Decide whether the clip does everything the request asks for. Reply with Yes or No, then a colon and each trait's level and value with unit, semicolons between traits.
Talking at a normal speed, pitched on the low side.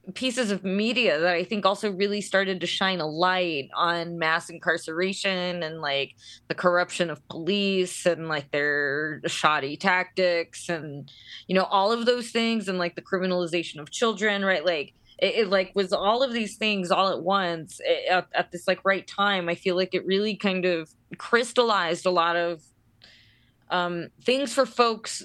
No: average, 180 wpm; medium, 180 Hz